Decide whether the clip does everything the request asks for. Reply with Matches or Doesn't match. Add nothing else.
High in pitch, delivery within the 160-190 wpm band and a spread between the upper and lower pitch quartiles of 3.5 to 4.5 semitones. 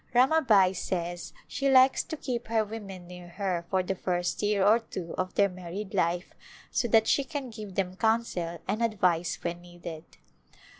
Matches